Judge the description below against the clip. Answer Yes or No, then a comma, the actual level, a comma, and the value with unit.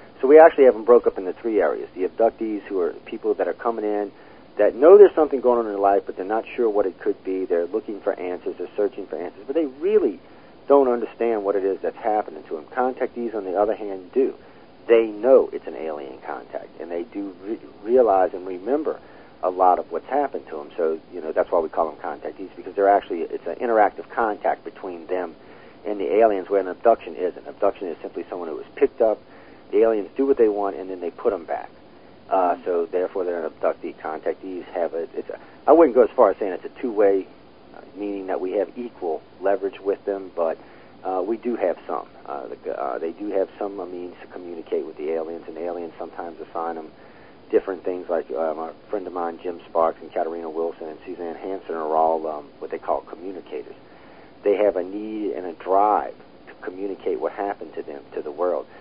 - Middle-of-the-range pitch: No, low, 120 Hz